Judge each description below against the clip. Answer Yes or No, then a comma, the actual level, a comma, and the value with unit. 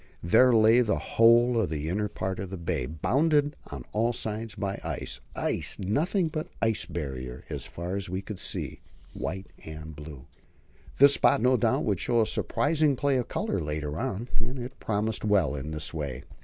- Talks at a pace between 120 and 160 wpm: No, average, 185 wpm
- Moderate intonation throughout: No, wide, 7.1 semitones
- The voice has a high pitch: No, low, 105 Hz